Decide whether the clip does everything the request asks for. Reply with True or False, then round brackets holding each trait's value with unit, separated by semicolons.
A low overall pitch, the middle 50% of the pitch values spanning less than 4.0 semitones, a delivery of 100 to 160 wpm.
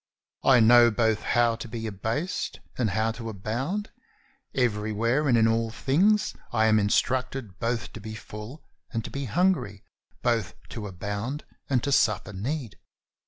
True (115 Hz; 3.3 semitones; 155 wpm)